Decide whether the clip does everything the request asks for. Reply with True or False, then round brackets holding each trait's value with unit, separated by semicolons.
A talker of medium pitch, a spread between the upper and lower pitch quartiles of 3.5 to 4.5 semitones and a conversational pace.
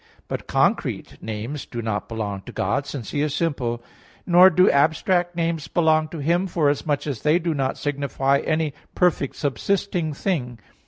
True (150 Hz; 4.0 semitones; 160 wpm)